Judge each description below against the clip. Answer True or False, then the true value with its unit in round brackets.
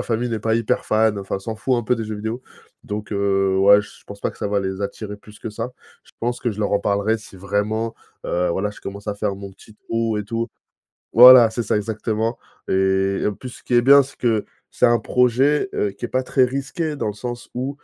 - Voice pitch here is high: False (110 Hz)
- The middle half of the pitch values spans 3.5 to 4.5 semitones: False (3.0 semitones)